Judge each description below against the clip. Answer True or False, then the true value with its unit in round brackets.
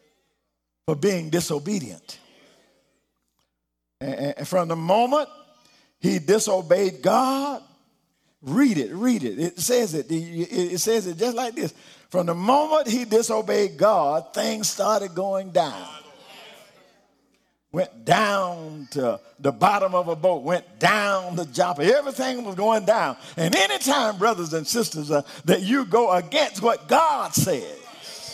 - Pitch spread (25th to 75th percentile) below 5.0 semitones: False (5.4 semitones)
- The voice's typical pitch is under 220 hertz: True (190 Hz)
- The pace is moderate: False (130 wpm)